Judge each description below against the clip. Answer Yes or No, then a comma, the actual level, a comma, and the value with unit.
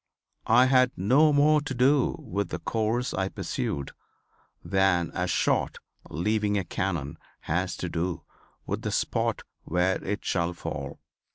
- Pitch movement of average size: No, wide, 6.1 semitones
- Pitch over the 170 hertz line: No, very low, 95 Hz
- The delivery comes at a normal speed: Yes, average, 145 wpm